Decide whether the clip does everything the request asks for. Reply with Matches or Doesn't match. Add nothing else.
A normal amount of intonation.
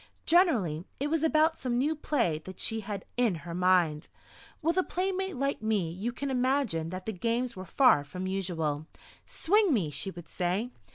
Doesn't match